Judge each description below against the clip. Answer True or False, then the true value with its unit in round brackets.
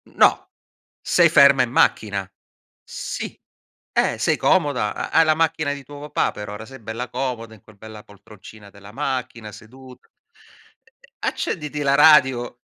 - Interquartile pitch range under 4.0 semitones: False (4.8 semitones)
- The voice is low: True (125 Hz)